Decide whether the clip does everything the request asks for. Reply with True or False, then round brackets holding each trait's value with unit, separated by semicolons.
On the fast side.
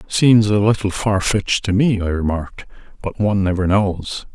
False (180 wpm)